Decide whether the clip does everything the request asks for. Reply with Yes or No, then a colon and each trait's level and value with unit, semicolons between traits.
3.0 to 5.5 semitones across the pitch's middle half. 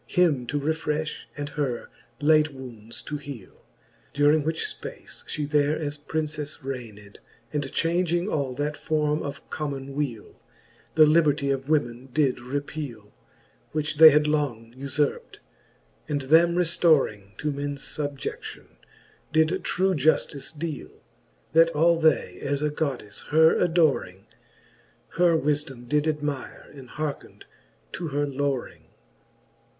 No: narrow, 2.4 semitones